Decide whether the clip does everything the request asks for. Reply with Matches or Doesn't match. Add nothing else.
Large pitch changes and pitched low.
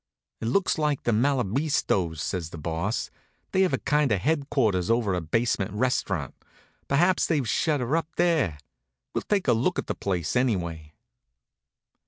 Matches